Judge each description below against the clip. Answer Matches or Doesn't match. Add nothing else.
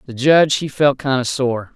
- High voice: Doesn't match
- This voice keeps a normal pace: Doesn't match